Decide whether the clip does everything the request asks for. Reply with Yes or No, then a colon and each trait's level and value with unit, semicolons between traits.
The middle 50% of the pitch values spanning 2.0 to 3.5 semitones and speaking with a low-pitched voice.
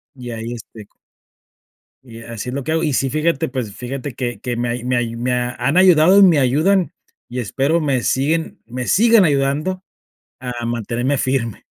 No: average, 4.2 semitones; low, 130 Hz